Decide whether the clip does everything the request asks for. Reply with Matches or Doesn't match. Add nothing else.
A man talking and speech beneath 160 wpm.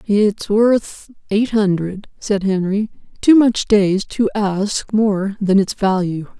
Doesn't match